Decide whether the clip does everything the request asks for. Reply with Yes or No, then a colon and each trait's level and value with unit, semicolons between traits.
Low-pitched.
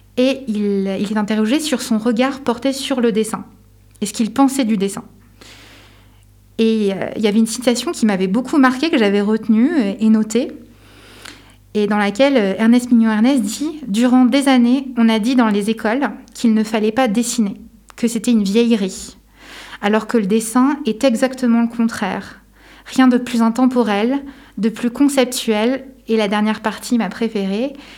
No: high, 230 Hz